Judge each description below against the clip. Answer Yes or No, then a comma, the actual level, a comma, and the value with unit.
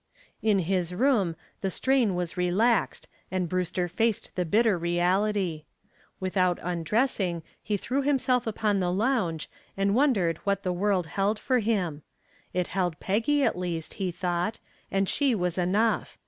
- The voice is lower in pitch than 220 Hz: Yes, high, 190 Hz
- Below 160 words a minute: Yes, average, 145 wpm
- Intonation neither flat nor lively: Yes, average, 3.9 semitones